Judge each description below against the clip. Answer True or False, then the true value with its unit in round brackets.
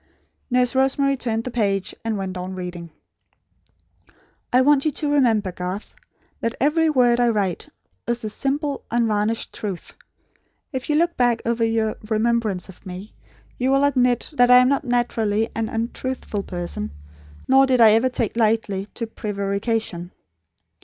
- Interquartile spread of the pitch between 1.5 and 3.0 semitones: False (3.8 semitones)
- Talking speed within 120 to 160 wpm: True (155 wpm)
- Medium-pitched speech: False (230 Hz)